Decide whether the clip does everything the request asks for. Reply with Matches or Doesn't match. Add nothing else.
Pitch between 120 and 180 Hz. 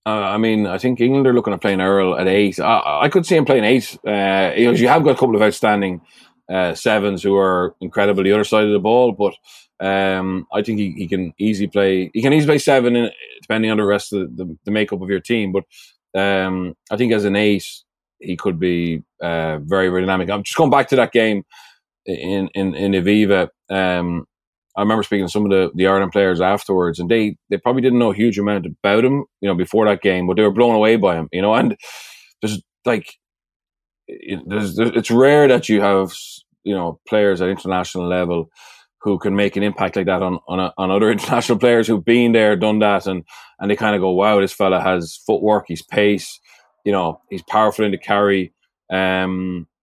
Doesn't match